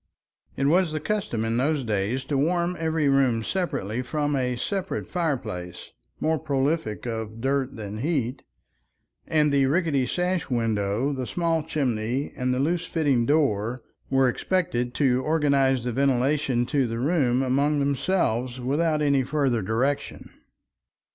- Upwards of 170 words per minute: No, average, 140 wpm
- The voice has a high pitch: No, low, 135 Hz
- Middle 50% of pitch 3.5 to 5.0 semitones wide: Yes, average, 4.1 semitones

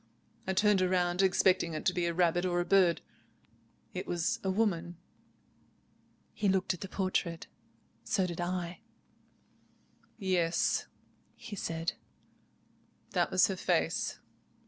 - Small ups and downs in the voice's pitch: Yes, narrow, 1.8 semitones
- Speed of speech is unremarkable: No, slow, 130 wpm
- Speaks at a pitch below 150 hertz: No, medium, 180 Hz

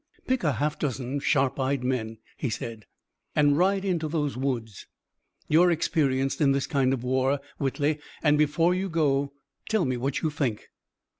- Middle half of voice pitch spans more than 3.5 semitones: No, average, 3.1 semitones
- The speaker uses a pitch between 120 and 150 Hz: Yes, medium, 140 Hz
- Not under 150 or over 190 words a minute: Yes, average, 165 wpm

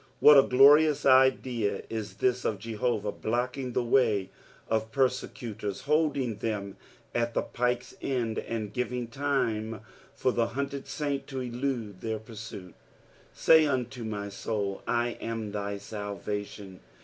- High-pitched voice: No, low, 115 Hz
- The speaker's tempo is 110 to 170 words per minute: Yes, average, 140 wpm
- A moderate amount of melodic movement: Yes, average, 3.6 semitones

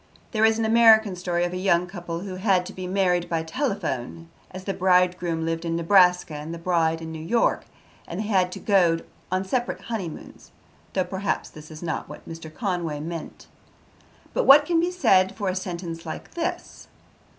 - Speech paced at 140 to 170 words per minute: No, average, 190 wpm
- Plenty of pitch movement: No, average, 3.2 semitones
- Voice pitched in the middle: Yes, medium, 180 Hz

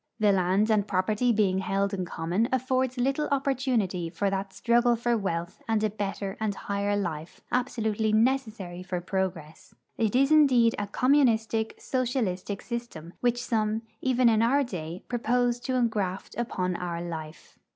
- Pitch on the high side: Yes, high, 215 Hz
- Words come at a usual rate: Yes, average, 150 wpm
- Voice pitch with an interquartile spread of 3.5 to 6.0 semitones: Yes, average, 4.4 semitones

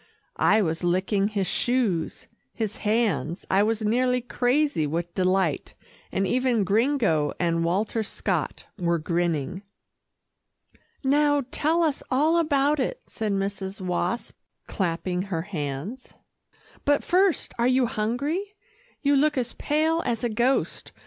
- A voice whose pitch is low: No, high, 215 Hz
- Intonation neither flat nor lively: No, wide, 6.8 semitones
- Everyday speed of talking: No, slow, 130 wpm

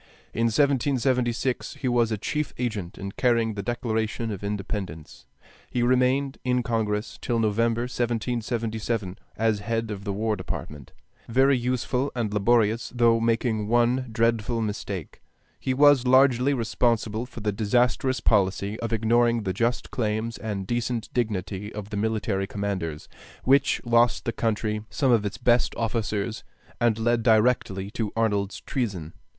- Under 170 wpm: Yes, average, 145 wpm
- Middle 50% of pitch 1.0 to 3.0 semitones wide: Yes, narrow, 2.6 semitones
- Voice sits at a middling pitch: No, low, 115 Hz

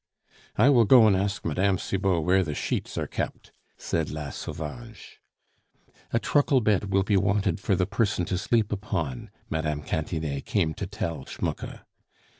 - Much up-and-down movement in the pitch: No, average, 4.8 semitones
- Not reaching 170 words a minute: Yes, average, 160 wpm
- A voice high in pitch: No, very low, 95 Hz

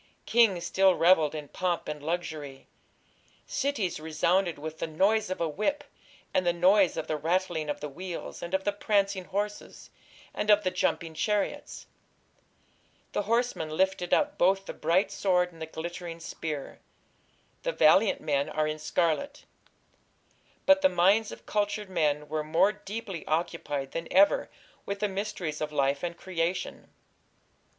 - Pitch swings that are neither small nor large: Yes, average, 4.2 semitones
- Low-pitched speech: No, medium, 180 Hz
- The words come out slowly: No, average, 155 wpm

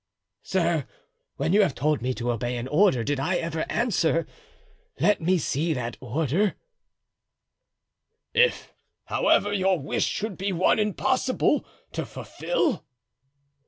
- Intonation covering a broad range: Yes, wide, 7.1 semitones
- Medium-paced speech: No, slow, 125 wpm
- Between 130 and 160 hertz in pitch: No, medium, 170 Hz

